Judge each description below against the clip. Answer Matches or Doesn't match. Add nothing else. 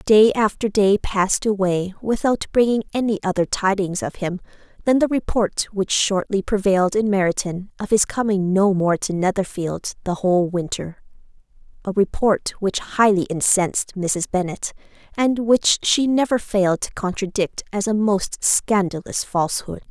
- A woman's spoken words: Matches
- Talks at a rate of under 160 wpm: Matches